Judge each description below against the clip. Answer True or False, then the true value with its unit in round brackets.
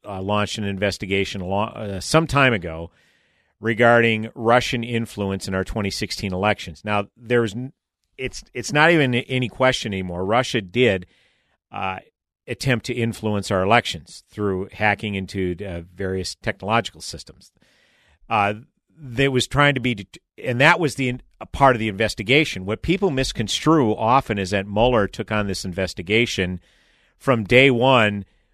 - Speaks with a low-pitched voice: True (110 Hz)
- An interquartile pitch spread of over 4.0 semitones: True (4.4 semitones)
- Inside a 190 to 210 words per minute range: False (155 wpm)